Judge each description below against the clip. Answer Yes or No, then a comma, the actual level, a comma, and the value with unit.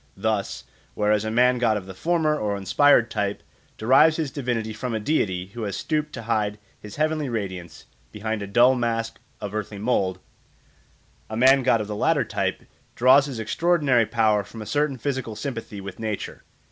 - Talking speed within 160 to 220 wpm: Yes, average, 180 wpm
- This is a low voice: Yes, low, 115 Hz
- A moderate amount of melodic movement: Yes, average, 4.0 semitones